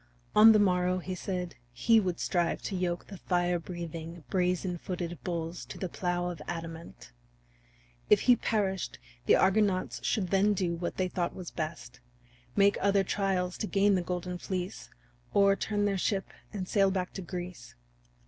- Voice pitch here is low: No, medium, 180 Hz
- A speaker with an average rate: Yes, average, 165 wpm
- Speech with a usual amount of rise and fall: No, narrow, 2.0 semitones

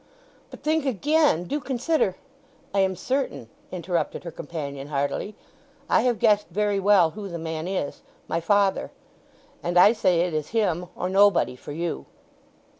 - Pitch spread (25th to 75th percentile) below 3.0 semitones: No, average, 4.1 semitones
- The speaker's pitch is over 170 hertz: Yes, medium, 185 Hz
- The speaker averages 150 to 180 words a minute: Yes, average, 155 wpm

